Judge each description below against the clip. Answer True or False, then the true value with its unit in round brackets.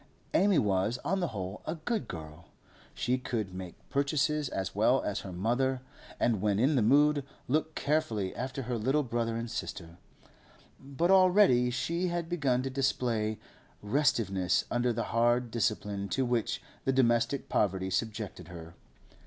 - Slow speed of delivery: False (155 wpm)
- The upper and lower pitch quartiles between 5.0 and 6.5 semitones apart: True (5.3 semitones)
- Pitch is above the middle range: False (120 Hz)